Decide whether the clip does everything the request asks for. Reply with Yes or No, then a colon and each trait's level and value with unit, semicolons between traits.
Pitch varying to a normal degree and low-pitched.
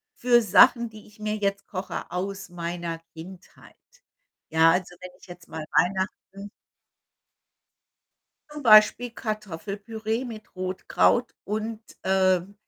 No: average, 3.1 semitones; high, 195 Hz